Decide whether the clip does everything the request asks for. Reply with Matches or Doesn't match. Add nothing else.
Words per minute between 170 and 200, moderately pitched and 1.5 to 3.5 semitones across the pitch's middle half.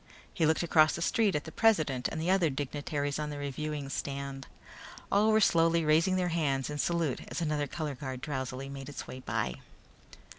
Matches